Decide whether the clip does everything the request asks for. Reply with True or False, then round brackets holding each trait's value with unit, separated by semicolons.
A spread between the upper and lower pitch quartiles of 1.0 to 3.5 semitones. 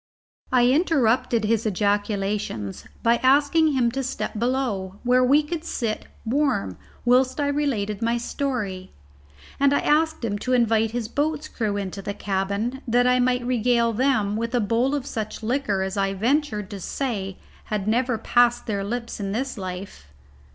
False (4.2 semitones)